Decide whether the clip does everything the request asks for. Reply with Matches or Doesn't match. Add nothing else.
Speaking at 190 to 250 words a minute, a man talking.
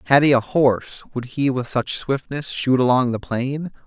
Matches